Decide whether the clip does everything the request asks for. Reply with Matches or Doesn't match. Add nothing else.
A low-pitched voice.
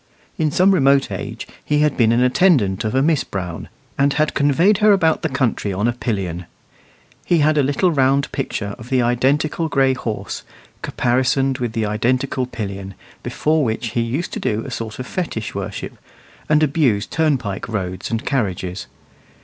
Matches